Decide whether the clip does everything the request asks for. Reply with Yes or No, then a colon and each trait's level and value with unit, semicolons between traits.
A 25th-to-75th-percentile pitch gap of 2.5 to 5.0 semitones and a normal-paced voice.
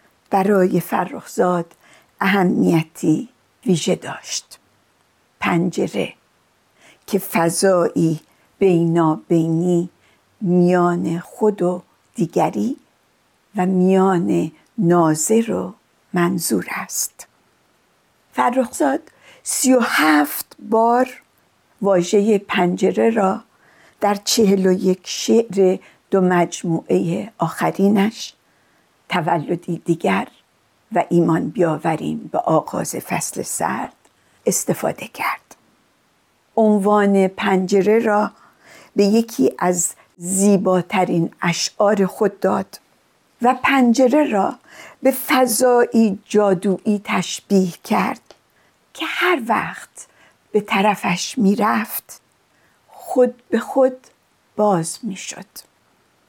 No: average, 4.1 semitones; slow, 80 wpm